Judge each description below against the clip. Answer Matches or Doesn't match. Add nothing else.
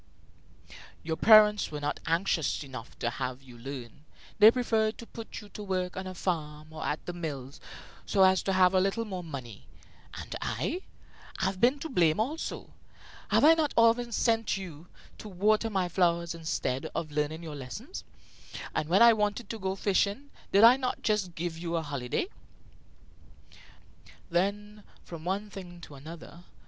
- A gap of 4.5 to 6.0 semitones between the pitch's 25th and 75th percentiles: Matches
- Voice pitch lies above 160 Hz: Matches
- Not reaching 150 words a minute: Doesn't match